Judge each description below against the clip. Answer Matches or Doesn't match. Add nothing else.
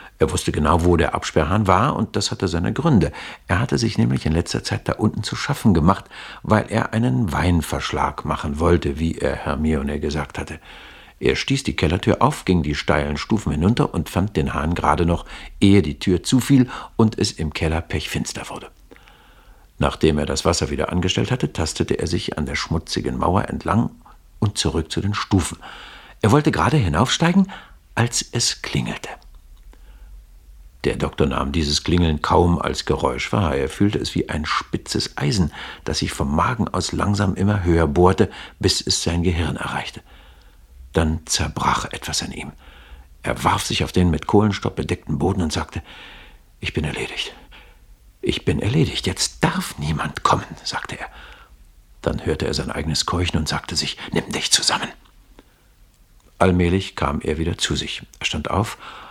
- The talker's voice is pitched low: Matches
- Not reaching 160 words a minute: Doesn't match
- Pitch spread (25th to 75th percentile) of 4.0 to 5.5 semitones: Matches